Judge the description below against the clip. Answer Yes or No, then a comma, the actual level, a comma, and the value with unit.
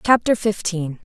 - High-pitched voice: Yes, high, 195 Hz